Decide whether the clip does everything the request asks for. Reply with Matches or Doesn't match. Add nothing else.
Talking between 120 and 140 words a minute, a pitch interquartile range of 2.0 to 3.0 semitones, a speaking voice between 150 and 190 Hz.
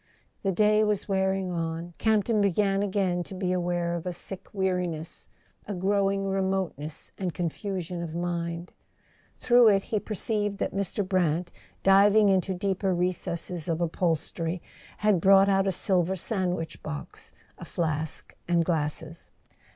Matches